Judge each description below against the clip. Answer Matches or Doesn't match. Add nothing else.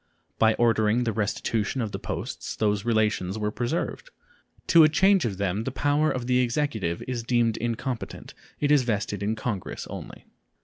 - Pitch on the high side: Doesn't match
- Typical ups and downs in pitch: Matches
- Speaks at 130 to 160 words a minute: Doesn't match